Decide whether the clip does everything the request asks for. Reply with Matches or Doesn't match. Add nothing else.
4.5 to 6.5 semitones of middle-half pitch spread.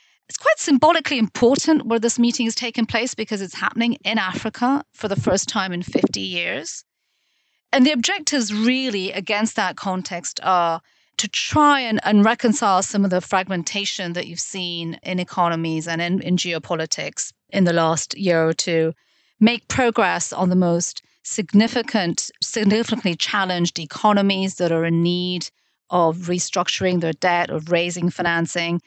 Matches